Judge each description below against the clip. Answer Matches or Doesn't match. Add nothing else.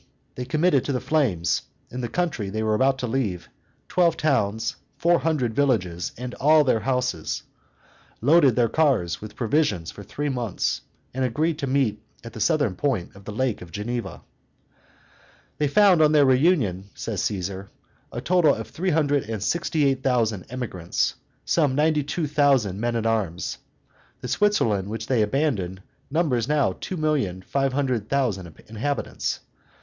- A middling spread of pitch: Doesn't match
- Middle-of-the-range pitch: Doesn't match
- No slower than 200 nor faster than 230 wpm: Doesn't match